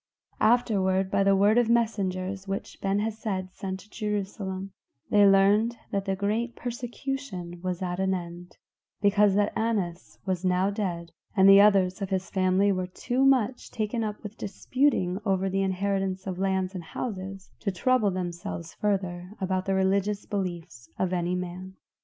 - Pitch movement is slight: Yes, narrow, 2.1 semitones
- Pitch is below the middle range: No, high, 195 Hz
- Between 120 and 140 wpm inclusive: No, average, 160 wpm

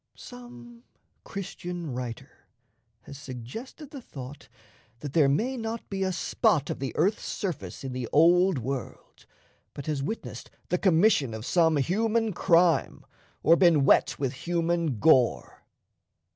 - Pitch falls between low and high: Yes, medium, 165 Hz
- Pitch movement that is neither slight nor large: No, wide, 6.4 semitones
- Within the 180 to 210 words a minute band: No, slow, 135 wpm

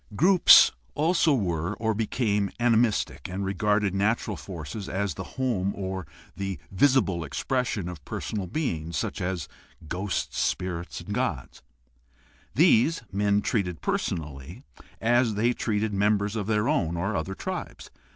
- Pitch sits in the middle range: No, low, 100 Hz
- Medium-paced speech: No, slow, 130 wpm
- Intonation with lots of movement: No, average, 3.9 semitones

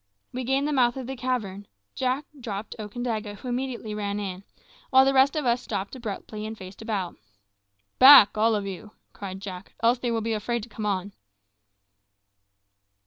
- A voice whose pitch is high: Yes, high, 225 Hz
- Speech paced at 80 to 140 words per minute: No, average, 175 wpm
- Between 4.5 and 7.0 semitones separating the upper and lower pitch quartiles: No, average, 3.8 semitones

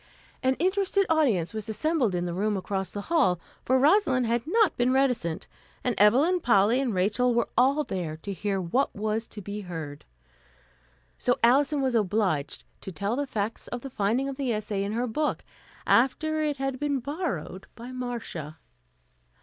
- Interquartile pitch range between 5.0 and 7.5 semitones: Yes, wide, 5.4 semitones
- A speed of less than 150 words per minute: No, average, 175 wpm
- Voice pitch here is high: Yes, high, 235 Hz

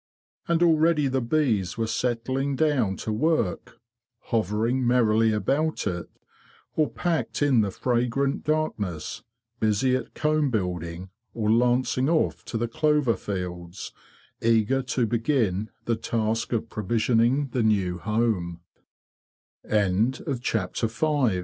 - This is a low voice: Yes, low, 115 Hz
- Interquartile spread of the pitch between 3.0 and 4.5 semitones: Yes, average, 4.1 semitones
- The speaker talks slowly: Yes, slow, 105 wpm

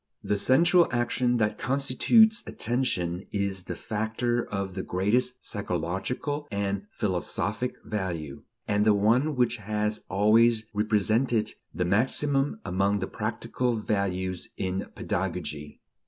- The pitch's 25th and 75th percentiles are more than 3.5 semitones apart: Yes, average, 4.2 semitones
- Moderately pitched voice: No, low, 105 Hz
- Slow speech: Yes, slow, 115 wpm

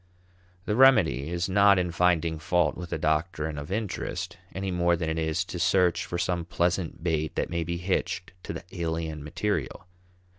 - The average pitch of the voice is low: Yes, very low, 85 Hz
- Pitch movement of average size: No, narrow, 2.3 semitones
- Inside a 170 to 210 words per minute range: Yes, average, 180 wpm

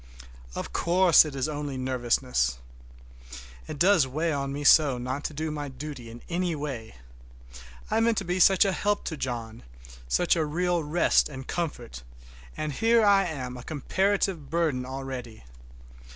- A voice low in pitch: No, medium, 150 Hz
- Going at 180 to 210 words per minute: No, average, 160 wpm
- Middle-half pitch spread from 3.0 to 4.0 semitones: No, average, 5.1 semitones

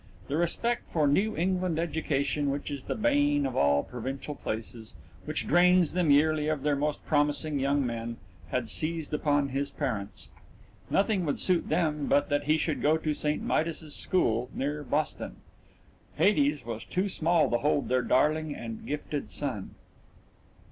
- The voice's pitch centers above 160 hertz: No, medium, 150 Hz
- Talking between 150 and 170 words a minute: Yes, average, 160 wpm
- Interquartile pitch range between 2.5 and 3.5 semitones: Yes, average, 3.1 semitones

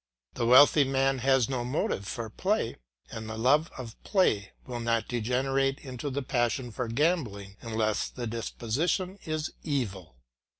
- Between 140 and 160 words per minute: Yes, average, 145 wpm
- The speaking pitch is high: No, low, 125 Hz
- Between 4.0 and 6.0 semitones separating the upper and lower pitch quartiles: No, average, 3.5 semitones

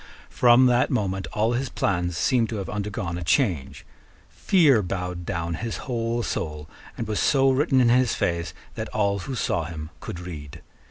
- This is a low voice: Yes, low, 105 Hz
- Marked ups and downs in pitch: Yes, wide, 5.8 semitones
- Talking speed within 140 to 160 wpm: No, average, 175 wpm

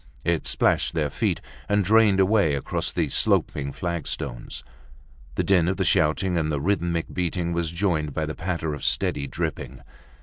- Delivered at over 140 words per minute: Yes, average, 165 wpm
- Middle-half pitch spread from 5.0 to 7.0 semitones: No, average, 3.4 semitones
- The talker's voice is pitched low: Yes, very low, 85 Hz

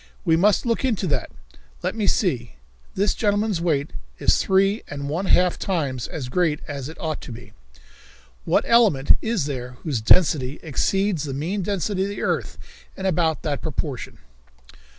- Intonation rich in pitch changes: Yes, wide, 5.7 semitones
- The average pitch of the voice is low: No, medium, 165 Hz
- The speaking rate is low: No, average, 165 wpm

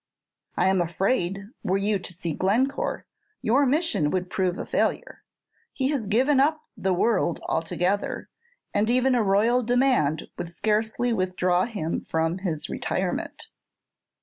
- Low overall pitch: No, high, 200 Hz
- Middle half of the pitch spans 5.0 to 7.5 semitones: Yes, wide, 5.4 semitones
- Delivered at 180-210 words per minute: No, average, 140 wpm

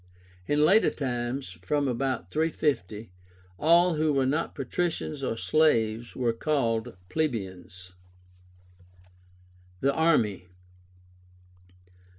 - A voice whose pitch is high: No, low, 135 Hz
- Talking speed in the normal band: No, slow, 90 wpm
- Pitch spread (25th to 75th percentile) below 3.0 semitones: No, wide, 5.5 semitones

